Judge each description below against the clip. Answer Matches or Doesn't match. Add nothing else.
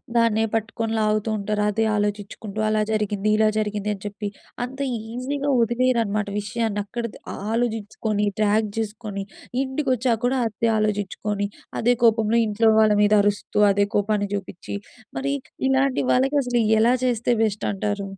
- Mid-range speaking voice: Doesn't match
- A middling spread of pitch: Doesn't match